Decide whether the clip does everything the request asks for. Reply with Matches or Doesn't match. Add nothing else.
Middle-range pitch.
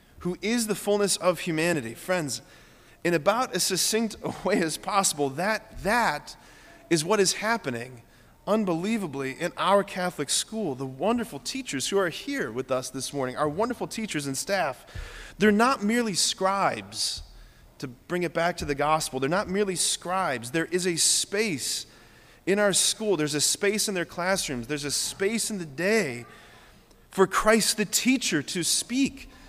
Matches